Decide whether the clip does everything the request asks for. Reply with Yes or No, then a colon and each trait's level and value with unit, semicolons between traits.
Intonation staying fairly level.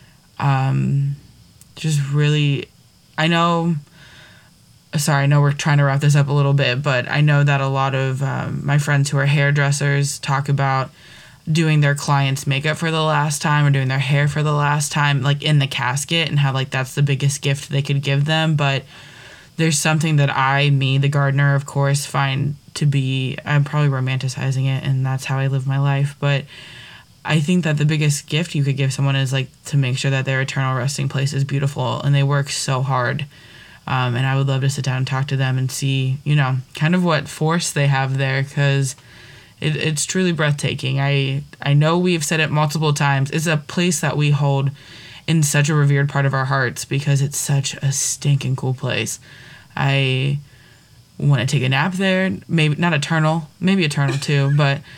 Yes: narrow, 1.6 semitones